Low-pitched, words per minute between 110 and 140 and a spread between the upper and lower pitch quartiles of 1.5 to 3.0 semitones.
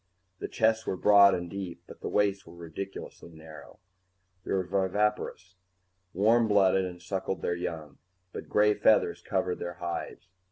No: very low, 95 Hz; average, 155 wpm; average, 2.7 semitones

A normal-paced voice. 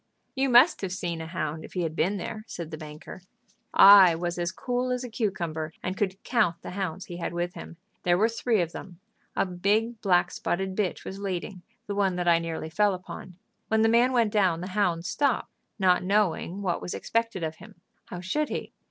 No: fast, 215 wpm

